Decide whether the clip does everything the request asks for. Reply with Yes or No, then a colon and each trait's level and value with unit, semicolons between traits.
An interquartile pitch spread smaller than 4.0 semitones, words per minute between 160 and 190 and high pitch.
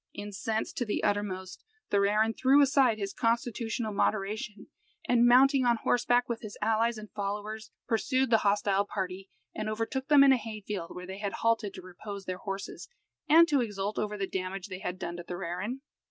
Yes: average, 3.2 semitones; average, 185 wpm; high, 215 Hz